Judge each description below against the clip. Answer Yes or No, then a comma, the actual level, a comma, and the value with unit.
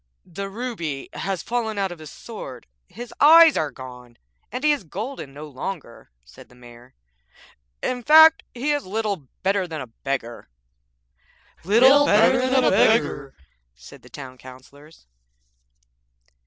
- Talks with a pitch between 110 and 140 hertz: No, high, 190 Hz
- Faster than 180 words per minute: No, average, 140 wpm